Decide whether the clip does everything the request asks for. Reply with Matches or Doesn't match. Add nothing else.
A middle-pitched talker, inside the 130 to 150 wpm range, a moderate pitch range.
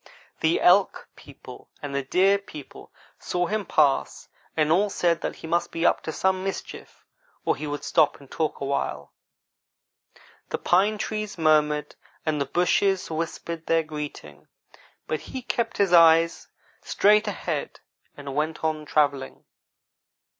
Matches